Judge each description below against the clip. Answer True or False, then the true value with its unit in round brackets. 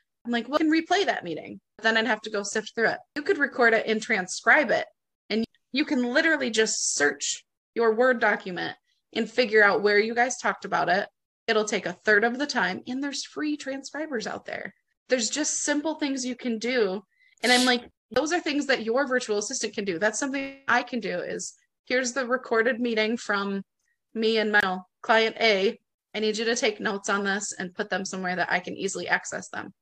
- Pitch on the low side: False (235 Hz)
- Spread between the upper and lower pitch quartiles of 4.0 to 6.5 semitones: True (4.4 semitones)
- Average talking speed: False (215 wpm)